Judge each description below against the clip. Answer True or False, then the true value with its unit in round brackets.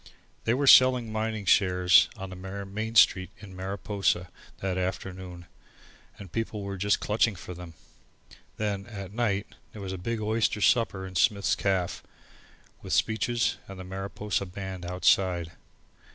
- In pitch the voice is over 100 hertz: False (95 Hz)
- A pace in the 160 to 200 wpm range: False (145 wpm)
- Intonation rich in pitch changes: False (2.6 semitones)